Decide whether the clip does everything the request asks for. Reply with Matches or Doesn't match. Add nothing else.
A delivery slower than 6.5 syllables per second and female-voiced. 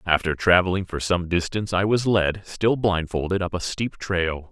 Doesn't match